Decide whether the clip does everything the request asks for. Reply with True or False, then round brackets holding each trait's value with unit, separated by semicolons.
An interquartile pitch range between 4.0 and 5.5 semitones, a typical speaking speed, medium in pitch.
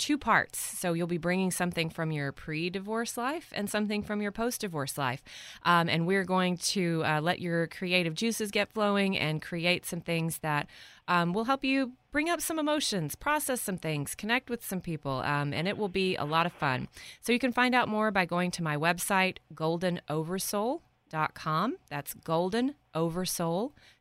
True (5.2 semitones; 185 wpm; 180 Hz)